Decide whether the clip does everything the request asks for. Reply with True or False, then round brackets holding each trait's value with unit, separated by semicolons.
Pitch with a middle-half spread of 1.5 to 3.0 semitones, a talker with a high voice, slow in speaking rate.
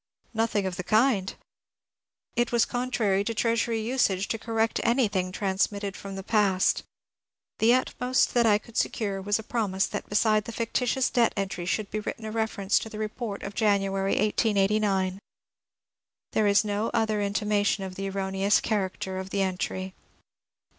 False (2.5 semitones; 210 Hz; 165 wpm)